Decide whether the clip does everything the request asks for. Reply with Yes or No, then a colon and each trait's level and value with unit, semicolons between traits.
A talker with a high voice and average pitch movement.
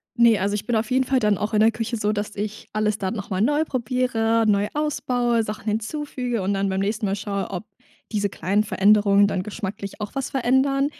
Yes: high, 215 Hz; average, 3.1 semitones